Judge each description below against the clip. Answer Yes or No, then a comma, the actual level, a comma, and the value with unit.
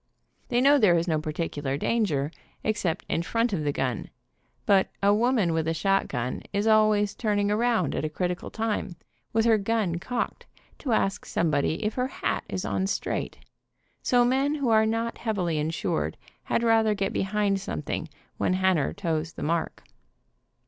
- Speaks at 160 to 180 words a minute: Yes, average, 170 wpm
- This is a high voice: Yes, high, 200 Hz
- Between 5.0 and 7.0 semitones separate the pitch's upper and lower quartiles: Yes, average, 5.3 semitones